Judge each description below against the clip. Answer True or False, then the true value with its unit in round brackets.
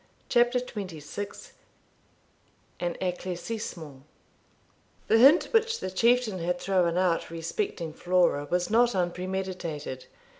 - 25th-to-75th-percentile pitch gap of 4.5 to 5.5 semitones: True (4.8 semitones)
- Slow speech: True (100 wpm)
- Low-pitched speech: False (185 Hz)